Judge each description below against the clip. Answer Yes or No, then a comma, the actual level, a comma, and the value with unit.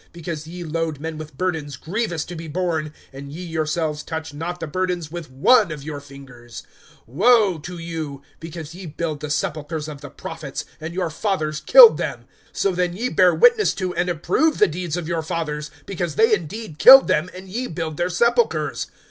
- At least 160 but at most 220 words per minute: Yes, average, 190 wpm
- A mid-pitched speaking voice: Yes, medium, 165 Hz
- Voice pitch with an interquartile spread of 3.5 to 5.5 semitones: No, average, 3.1 semitones